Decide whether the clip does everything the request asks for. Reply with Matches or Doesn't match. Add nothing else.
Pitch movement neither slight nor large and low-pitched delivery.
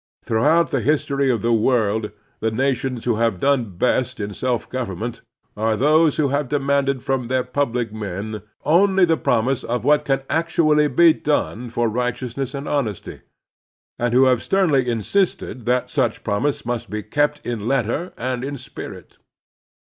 Matches